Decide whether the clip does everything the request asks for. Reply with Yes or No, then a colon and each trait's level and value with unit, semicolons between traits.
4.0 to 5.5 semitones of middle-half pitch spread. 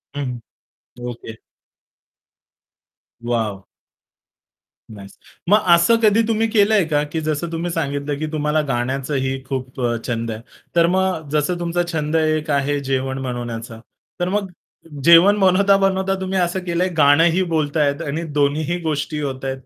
Yes: average, 4.7 semitones